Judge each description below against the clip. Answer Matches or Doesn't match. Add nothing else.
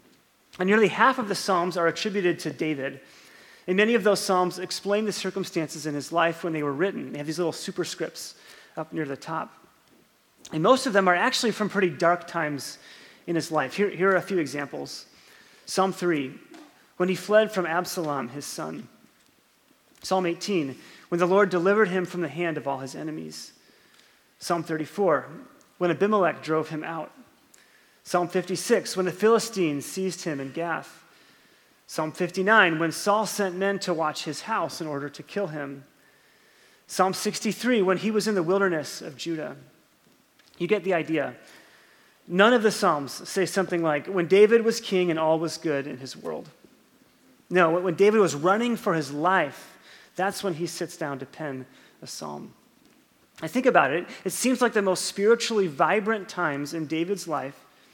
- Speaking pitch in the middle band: Matches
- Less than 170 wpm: Doesn't match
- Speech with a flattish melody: Doesn't match